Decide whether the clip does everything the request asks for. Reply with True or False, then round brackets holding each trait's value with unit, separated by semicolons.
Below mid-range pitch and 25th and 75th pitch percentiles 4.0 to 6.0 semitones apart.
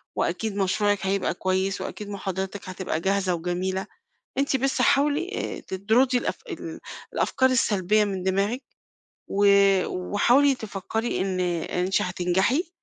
False (200 Hz; 4.7 semitones)